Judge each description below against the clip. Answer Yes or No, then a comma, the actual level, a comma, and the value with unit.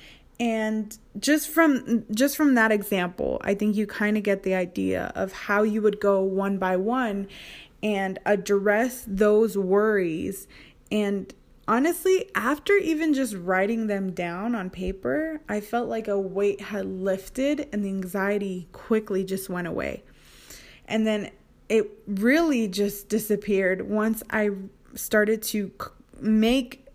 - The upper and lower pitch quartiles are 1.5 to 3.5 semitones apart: Yes, average, 2.7 semitones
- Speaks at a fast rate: No, average, 140 wpm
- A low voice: No, high, 210 Hz